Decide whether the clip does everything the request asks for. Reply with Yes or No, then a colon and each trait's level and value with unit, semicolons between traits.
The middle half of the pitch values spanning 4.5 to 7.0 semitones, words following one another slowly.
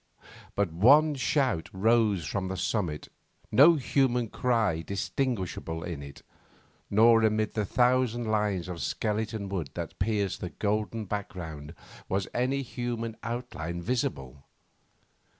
Yes: average, 4.9 semitones; slow, 120 wpm